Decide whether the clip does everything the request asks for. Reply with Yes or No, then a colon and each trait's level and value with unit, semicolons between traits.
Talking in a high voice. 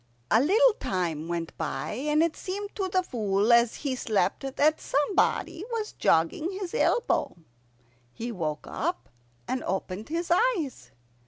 Yes: very high, 270 Hz